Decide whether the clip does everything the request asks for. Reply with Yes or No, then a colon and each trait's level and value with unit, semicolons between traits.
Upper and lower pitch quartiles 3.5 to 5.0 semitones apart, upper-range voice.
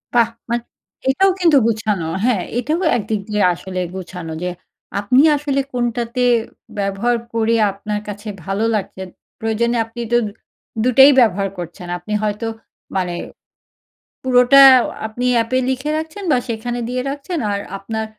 Yes: average, 3.8 semitones; high, 230 Hz